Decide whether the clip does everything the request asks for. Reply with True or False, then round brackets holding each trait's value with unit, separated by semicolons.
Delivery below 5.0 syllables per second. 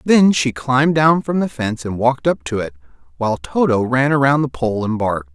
False (5.6 syllables/s)